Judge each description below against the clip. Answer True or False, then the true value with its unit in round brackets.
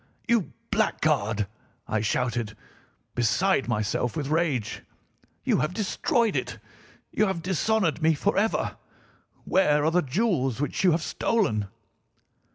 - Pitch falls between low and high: True (155 Hz)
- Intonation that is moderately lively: False (7.9 semitones)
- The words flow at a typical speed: False (120 wpm)